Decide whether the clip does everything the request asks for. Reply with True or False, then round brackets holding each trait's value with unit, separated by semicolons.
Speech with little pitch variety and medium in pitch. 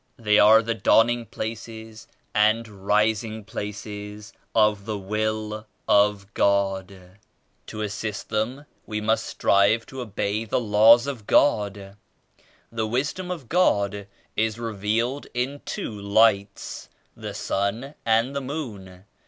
False (2.1 semitones; 110 Hz)